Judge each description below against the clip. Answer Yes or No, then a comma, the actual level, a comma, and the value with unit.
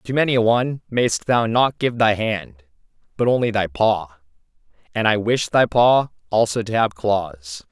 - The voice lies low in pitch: Yes, low, 110 Hz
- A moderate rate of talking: Yes, average, 180 wpm